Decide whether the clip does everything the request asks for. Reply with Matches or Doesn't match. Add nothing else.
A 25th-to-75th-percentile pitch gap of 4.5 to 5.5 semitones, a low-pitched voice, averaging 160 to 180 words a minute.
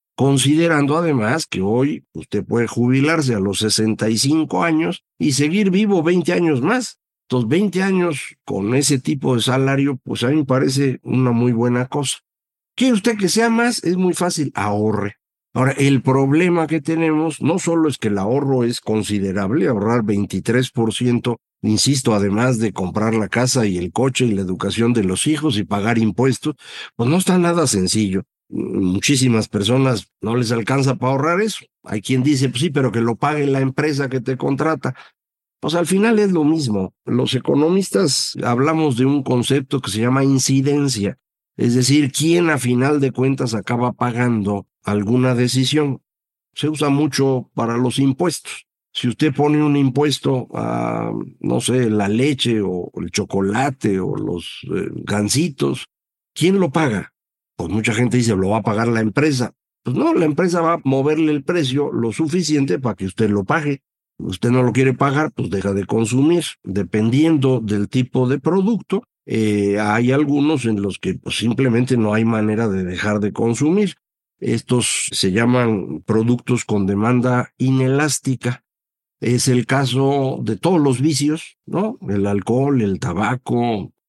Matches